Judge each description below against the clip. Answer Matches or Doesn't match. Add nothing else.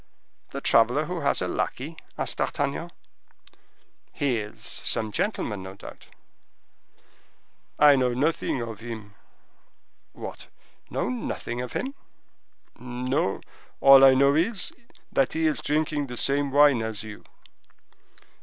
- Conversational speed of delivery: Doesn't match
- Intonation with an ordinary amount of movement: Matches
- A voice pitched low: Matches